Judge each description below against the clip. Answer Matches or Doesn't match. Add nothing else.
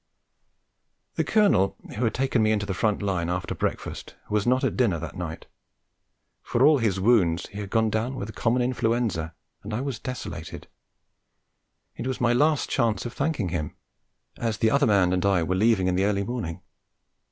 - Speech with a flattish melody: Doesn't match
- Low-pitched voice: Matches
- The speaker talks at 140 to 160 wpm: Doesn't match